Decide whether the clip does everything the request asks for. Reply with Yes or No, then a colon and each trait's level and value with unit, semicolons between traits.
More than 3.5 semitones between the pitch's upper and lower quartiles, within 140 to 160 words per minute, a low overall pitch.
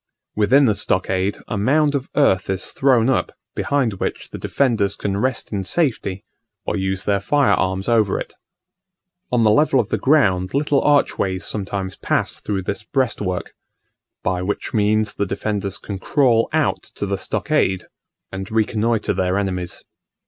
Yes: average, 4.7 semitones; average, 155 wpm; low, 105 Hz